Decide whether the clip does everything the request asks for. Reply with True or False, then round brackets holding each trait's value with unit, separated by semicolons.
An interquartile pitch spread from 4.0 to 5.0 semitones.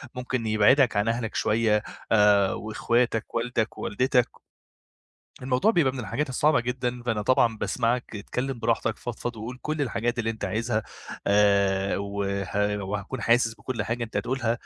False (2.8 semitones)